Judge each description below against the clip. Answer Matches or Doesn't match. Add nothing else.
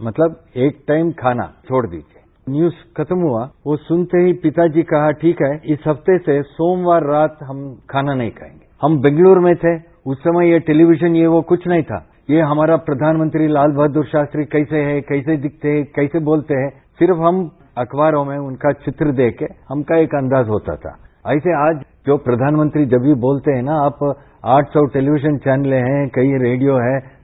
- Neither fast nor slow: Matches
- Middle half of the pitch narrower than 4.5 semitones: Matches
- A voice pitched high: Doesn't match